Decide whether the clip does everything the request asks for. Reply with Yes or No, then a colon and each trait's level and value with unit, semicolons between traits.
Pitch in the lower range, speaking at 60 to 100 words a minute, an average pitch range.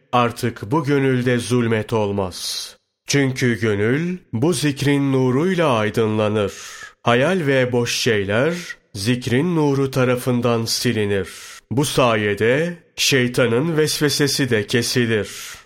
Yes: low, 125 Hz; slow, 95 wpm; average, 3.9 semitones